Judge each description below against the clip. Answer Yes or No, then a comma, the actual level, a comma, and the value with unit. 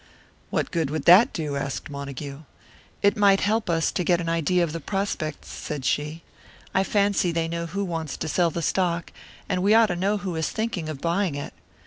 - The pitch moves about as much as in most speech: Yes, average, 4.0 semitones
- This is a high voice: No, medium, 170 Hz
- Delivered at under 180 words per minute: No, fast, 205 wpm